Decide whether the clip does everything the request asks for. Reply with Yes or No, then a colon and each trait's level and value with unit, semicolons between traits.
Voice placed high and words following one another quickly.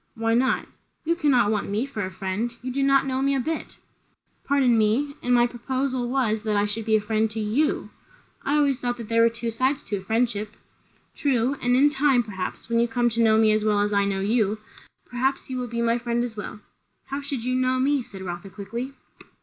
Yes: high, 235 Hz; fast, 225 wpm